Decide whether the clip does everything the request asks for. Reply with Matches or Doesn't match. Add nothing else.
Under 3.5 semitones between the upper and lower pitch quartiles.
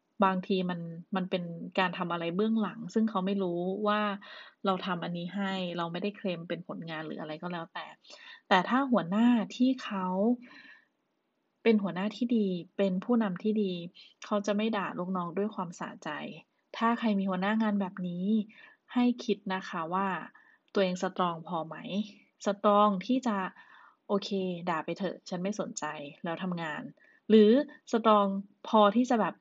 Matches